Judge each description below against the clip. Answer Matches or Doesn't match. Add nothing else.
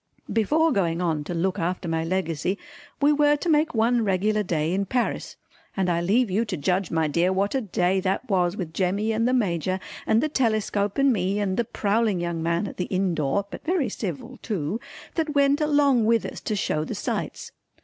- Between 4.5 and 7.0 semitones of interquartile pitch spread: Matches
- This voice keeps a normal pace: Doesn't match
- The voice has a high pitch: Matches